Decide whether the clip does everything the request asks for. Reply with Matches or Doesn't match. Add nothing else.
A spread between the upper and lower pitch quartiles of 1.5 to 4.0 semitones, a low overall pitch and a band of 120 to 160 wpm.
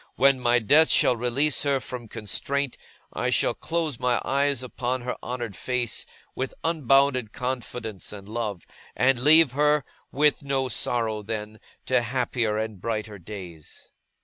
Matches